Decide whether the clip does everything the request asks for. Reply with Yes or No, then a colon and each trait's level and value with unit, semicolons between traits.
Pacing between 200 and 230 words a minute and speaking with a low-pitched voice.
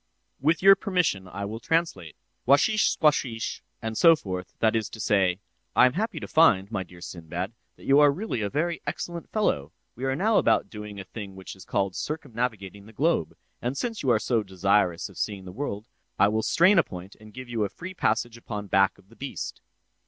Yes: fast, 205 wpm; low, 110 Hz